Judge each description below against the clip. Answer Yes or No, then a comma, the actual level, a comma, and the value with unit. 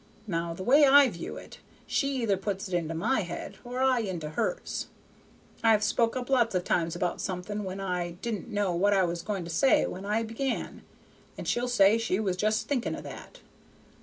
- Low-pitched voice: No, high, 205 Hz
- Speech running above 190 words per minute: Yes, average, 200 wpm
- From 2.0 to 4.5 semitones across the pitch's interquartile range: No, average, 5.0 semitones